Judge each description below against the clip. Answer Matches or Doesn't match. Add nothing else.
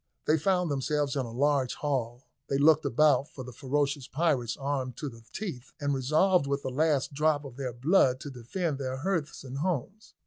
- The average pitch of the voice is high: Doesn't match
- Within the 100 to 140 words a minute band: Doesn't match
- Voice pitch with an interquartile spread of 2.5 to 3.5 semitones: Matches